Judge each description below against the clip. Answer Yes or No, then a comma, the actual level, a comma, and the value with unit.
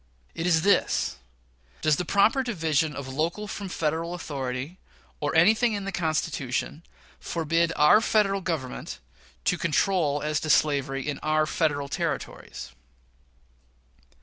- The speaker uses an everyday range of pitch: Yes, average, 4.0 semitones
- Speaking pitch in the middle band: Yes, medium, 160 Hz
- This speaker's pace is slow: Yes, slow, 125 wpm